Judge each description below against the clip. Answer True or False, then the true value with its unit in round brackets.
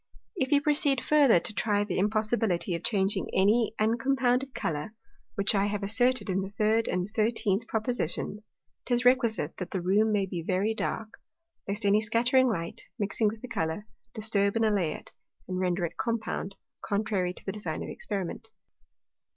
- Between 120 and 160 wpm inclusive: False (170 wpm)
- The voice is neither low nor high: False (210 Hz)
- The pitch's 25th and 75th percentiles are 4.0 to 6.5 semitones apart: False (3.1 semitones)